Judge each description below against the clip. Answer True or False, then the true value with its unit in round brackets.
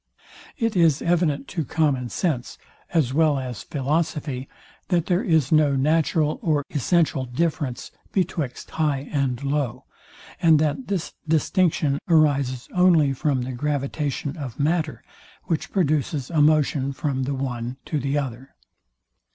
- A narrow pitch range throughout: False (3.1 semitones)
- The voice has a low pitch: False (150 Hz)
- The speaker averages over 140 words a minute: False (135 wpm)